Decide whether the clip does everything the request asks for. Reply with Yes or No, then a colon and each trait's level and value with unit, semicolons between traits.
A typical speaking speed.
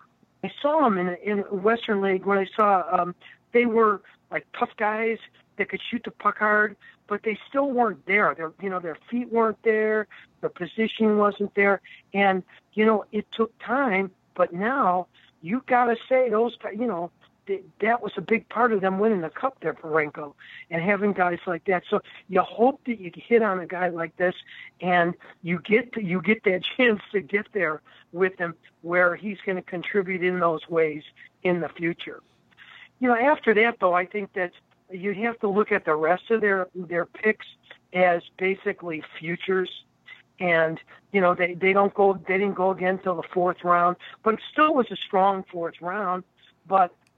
Yes: average, 195 wpm